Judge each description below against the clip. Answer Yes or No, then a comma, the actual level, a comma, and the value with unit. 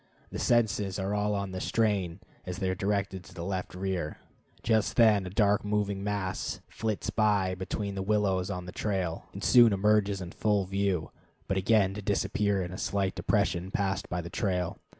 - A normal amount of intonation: No, narrow, 1.9 semitones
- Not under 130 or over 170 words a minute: No, average, 190 wpm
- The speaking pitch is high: No, low, 100 Hz